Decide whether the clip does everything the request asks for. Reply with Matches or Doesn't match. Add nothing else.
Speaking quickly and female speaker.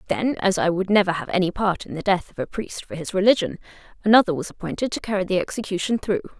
Matches